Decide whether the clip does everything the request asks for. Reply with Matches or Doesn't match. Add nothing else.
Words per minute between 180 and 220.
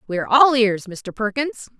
Matches